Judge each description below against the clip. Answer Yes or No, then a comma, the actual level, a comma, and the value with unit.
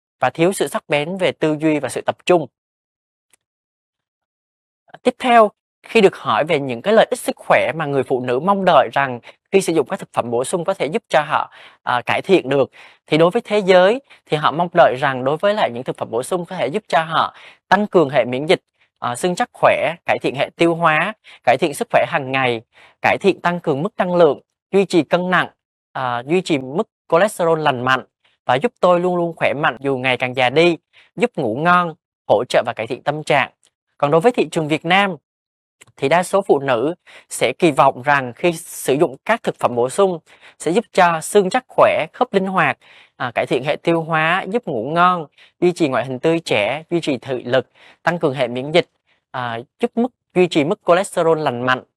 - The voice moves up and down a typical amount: No, wide, 5.7 semitones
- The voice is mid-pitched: Yes, medium, 170 Hz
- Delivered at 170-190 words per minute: No, average, 225 wpm